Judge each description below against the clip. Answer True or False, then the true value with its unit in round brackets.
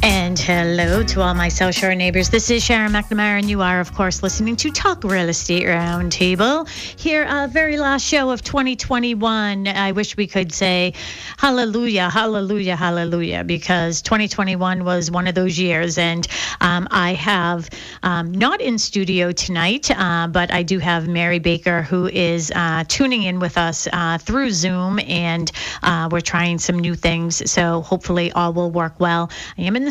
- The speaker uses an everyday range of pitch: True (3.4 semitones)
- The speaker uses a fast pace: False (175 wpm)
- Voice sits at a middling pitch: True (180 Hz)